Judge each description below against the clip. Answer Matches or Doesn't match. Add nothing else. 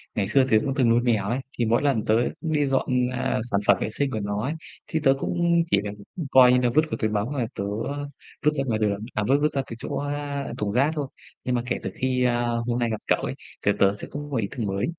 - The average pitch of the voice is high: Doesn't match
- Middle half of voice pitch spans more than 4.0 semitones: Matches